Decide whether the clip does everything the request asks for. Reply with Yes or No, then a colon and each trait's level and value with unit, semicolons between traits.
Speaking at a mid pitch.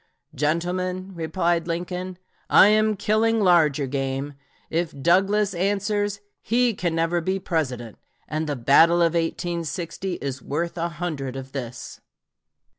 Yes: medium, 170 Hz